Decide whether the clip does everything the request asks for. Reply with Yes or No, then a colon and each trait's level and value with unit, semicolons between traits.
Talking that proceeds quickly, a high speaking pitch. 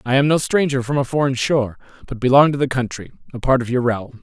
No: fast, 255 wpm; low, 130 Hz